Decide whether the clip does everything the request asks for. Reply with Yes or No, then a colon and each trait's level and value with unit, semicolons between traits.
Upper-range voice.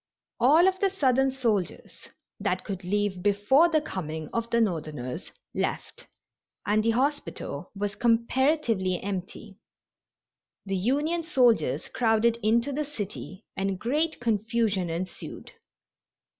Yes: high, 225 Hz